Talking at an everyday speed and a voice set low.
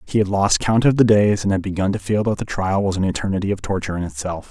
No: fast, 295 wpm; low, 100 Hz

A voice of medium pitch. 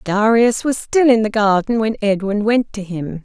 No: high, 215 Hz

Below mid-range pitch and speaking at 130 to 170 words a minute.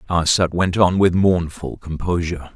Yes: very low, 85 Hz; average, 140 wpm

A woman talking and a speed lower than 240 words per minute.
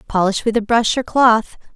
Yes: female; fast, 205 wpm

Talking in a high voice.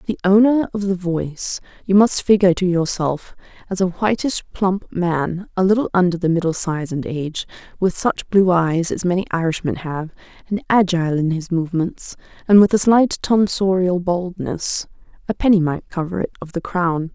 No: medium, 180 Hz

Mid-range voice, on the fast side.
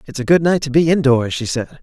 Yes: medium, 145 Hz; fast, 295 wpm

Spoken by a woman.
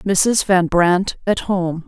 Yes: female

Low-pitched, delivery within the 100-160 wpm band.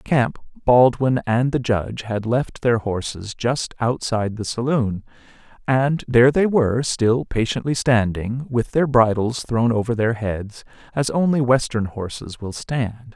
Yes: low, 120 Hz; average, 150 wpm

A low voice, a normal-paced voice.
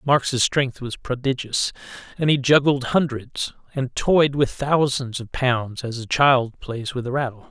Yes: low, 130 Hz; average, 170 wpm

